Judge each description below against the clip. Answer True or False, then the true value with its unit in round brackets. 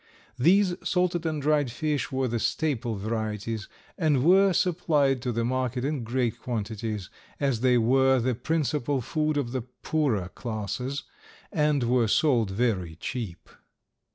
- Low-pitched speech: True (130 Hz)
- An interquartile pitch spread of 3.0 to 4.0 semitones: False (4.7 semitones)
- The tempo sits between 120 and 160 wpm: True (140 wpm)